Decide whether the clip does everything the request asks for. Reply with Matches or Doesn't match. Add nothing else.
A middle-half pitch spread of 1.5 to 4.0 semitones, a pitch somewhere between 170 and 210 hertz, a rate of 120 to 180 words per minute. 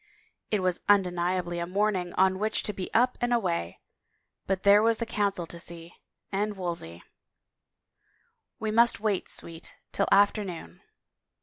Matches